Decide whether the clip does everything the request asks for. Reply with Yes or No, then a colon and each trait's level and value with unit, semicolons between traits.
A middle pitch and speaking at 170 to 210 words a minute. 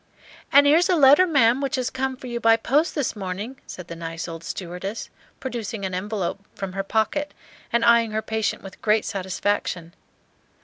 No: high, 220 Hz; average, 180 wpm